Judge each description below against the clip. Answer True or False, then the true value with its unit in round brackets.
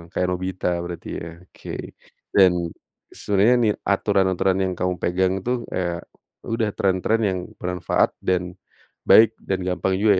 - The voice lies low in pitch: True (95 Hz)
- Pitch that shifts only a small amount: True (1.8 semitones)